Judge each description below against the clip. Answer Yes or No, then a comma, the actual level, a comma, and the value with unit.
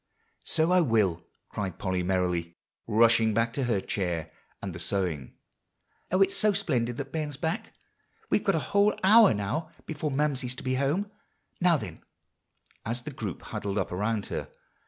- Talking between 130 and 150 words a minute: No, average, 165 wpm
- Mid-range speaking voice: No, low, 115 Hz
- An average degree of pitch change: No, wide, 8.1 semitones